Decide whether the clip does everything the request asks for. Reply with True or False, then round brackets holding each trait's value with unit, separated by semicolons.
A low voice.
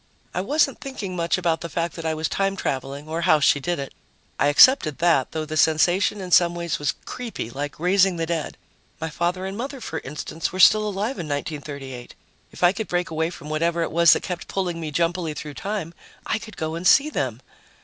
False (170 Hz)